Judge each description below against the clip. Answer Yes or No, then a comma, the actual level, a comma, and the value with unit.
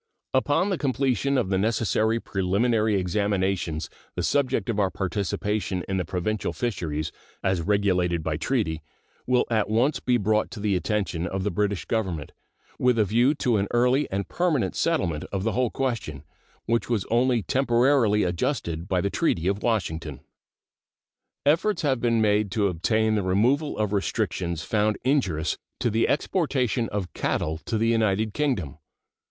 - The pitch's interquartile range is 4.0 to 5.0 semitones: Yes, average, 4.6 semitones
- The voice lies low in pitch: Yes, low, 105 Hz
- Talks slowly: No, average, 160 wpm